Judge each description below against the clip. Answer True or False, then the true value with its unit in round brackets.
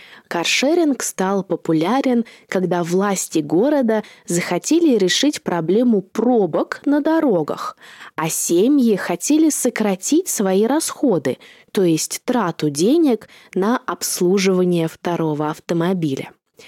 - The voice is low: False (200 Hz)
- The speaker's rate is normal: False (95 wpm)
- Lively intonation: True (6.6 semitones)